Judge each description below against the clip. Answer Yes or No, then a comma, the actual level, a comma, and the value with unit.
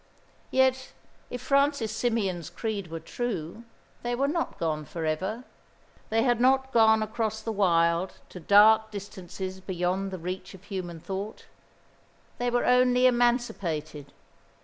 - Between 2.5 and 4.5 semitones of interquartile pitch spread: No, average, 5.1 semitones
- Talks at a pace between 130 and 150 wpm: Yes, slow, 135 wpm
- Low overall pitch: No, high, 215 Hz